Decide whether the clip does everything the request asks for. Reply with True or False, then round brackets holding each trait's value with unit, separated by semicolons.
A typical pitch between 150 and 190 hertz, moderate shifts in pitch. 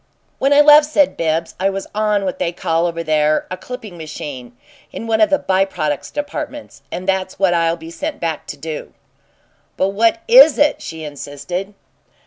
False (185 Hz; 6.0 semitones)